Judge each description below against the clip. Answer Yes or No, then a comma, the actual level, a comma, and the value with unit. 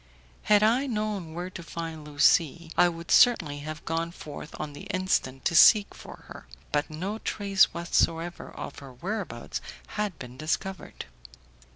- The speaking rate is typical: Yes, average, 155 wpm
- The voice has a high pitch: No, medium, 170 Hz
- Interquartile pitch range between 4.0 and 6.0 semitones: Yes, average, 4.4 semitones